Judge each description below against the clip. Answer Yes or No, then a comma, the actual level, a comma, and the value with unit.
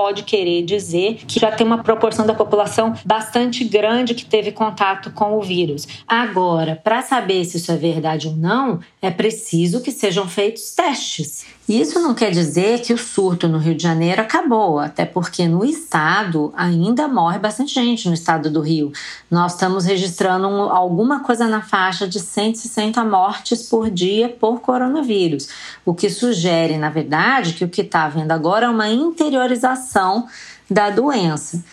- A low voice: No, high, 205 Hz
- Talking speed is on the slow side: No, average, 165 wpm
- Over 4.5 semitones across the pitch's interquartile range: Yes, average, 5.0 semitones